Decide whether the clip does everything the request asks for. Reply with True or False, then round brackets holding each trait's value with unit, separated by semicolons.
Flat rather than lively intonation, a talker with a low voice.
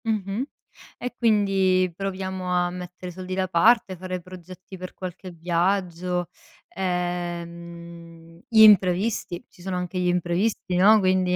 False (1.5 semitones; 185 Hz)